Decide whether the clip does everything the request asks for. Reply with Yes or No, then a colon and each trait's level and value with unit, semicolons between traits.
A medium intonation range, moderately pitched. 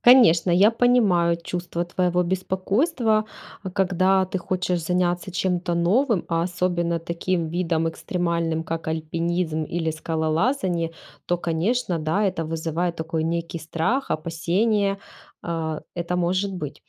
No: narrow, 2.3 semitones; medium, 175 Hz